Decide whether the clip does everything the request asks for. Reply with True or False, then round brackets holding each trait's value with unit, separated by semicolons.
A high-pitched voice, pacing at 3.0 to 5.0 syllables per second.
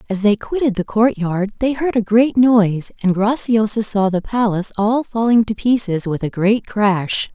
True (215 Hz; 4.6 syllables/s)